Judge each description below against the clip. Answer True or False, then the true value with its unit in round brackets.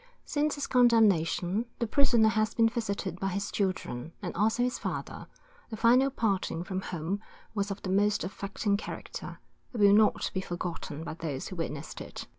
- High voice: True (200 Hz)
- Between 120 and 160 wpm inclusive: False (175 wpm)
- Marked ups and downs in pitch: False (3.8 semitones)